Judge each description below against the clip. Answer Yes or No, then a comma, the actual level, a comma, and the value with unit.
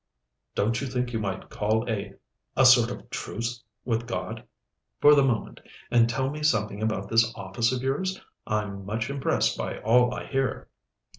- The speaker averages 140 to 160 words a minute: No, average, 170 wpm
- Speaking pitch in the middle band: No, low, 115 Hz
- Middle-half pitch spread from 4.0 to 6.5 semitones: No, average, 3.4 semitones